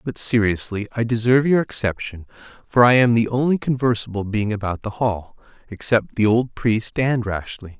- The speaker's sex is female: No, male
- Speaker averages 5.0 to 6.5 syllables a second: Yes, 5.2 syllables/s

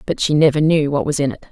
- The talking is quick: Yes, fast, 315 wpm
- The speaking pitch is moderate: Yes, medium, 145 Hz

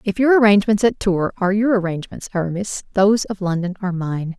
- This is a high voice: Yes, high, 195 Hz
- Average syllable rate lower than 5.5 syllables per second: No, 6.5 syllables/s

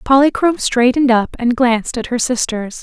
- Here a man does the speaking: No, female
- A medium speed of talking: Yes, average, 170 wpm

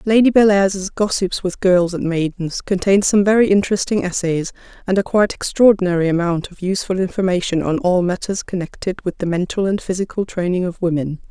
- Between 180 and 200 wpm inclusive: No, average, 170 wpm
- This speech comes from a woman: Yes, female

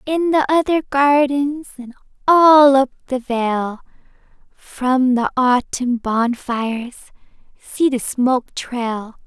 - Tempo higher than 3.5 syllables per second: No, 3.3 syllables/s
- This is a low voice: No, very high, 260 Hz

